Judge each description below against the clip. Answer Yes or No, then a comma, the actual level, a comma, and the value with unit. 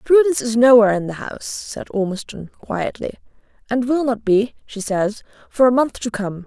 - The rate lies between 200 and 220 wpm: No, average, 185 wpm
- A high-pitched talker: Yes, high, 230 Hz